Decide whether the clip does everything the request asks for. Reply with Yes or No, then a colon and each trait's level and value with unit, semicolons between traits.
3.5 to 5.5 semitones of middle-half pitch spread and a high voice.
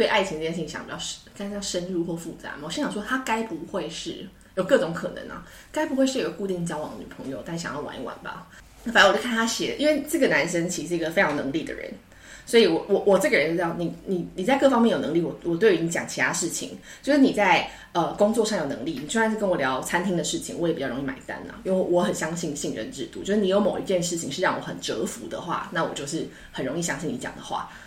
Yes: average, 5.2 semitones; high, 195 Hz